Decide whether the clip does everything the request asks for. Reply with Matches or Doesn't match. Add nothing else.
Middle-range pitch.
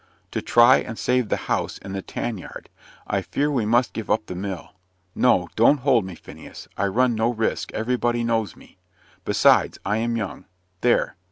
Doesn't match